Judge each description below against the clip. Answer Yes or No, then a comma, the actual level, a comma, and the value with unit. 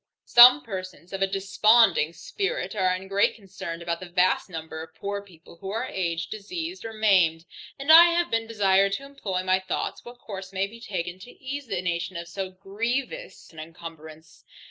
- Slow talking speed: No, average, 190 wpm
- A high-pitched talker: Yes, high, 195 Hz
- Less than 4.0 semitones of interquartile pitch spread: No, average, 4.5 semitones